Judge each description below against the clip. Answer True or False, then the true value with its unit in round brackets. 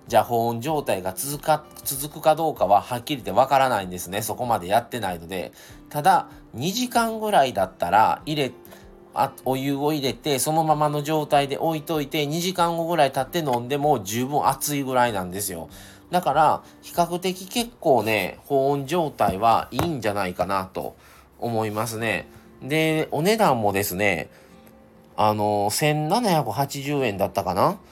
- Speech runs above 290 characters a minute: True (315 characters per minute)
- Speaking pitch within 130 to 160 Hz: True (140 Hz)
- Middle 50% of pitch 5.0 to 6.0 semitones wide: False (6.8 semitones)